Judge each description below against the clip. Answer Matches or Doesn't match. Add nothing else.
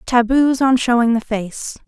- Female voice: Matches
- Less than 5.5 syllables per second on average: Matches